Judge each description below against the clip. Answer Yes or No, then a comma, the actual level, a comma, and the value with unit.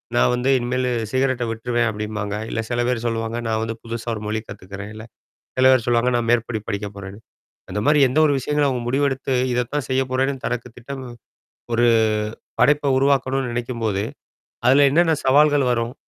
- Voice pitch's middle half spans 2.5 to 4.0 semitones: Yes, average, 2.8 semitones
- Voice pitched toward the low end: Yes, low, 120 Hz